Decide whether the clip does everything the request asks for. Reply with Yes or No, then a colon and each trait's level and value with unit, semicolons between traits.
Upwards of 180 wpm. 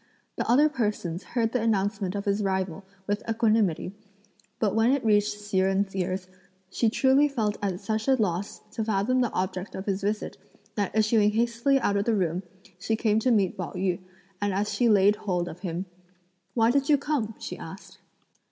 Yes: average, 190 wpm